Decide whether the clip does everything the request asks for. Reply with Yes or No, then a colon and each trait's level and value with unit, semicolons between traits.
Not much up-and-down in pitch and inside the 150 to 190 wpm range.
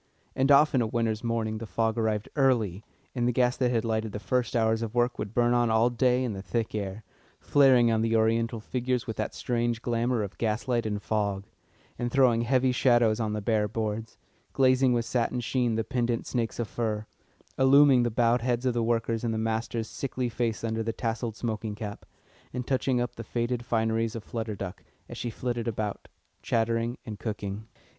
No: narrow, 1.7 semitones; average, 200 wpm